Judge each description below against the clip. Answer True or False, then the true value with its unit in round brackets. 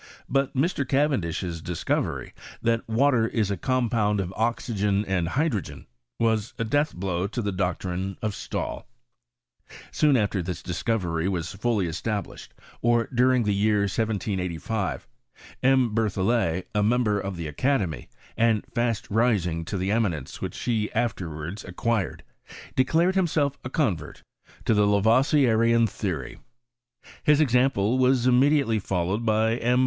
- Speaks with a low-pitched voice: True (110 Hz)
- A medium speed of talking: False (125 wpm)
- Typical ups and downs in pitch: True (4.4 semitones)